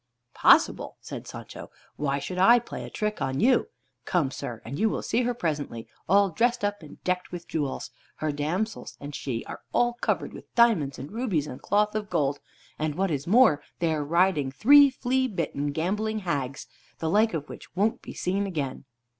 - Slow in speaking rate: No, average, 190 wpm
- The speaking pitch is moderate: Yes, medium, 180 Hz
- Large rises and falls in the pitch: Yes, wide, 6.8 semitones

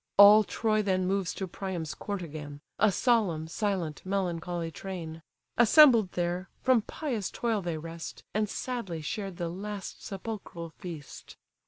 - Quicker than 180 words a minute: No, average, 140 wpm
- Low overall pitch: No, high, 190 Hz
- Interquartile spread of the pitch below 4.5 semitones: Yes, average, 4.0 semitones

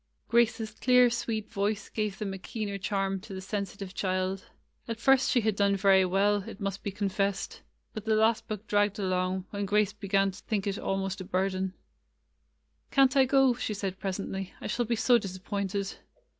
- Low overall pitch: No, high, 200 Hz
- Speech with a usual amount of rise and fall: No, narrow, 2.1 semitones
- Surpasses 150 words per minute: Yes, average, 185 wpm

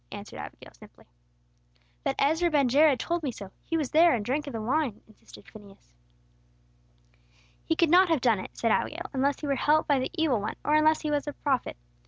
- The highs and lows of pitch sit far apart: No, average, 4.1 semitones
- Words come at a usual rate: No, fast, 210 wpm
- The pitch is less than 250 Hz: No, very high, 285 Hz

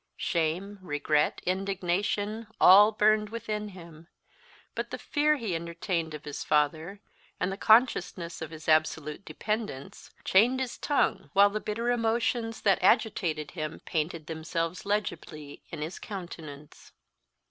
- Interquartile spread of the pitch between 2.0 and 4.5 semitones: No, average, 5.0 semitones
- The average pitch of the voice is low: No, medium, 185 Hz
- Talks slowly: Yes, slow, 130 wpm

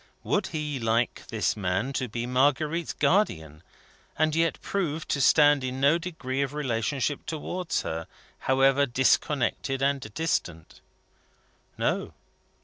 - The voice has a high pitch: No, low, 135 Hz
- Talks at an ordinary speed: No, slow, 125 wpm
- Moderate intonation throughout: Yes, average, 4.1 semitones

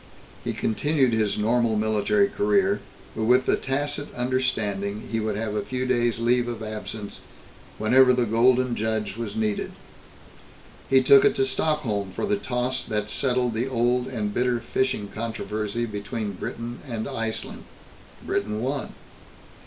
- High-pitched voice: No, low, 120 Hz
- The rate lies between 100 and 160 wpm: Yes, average, 145 wpm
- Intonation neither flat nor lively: Yes, average, 3.0 semitones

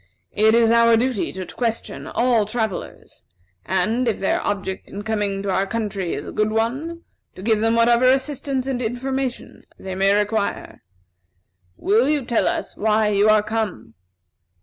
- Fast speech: No, average, 160 wpm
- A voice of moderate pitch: No, high, 220 Hz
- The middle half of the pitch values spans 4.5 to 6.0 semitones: No, average, 3.0 semitones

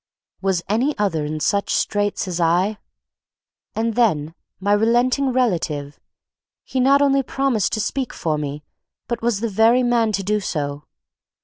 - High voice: Yes, high, 210 Hz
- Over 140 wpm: Yes, average, 150 wpm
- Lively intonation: Yes, wide, 6.1 semitones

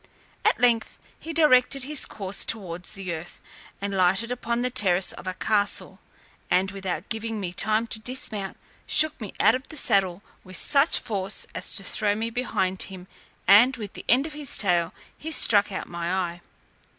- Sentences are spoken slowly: No, average, 180 wpm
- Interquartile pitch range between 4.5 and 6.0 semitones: Yes, average, 4.8 semitones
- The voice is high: Yes, high, 210 Hz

